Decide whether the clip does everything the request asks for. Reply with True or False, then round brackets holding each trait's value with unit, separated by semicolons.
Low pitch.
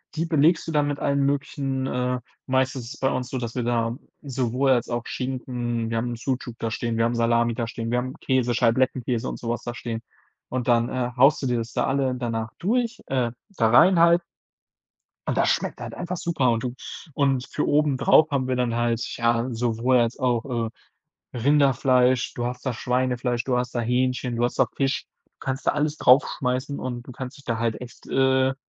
True (125 Hz)